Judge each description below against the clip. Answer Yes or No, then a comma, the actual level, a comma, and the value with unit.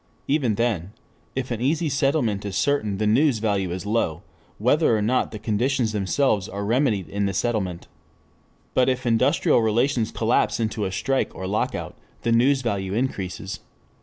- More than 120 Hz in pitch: No, low, 110 Hz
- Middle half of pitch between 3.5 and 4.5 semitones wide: Yes, average, 4.2 semitones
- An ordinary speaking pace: Yes, average, 165 wpm